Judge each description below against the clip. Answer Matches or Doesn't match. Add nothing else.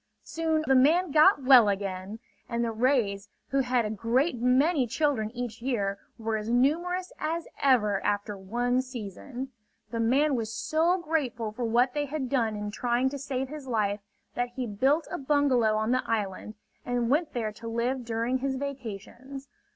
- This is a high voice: Matches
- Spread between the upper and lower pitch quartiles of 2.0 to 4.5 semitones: Matches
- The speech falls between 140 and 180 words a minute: Matches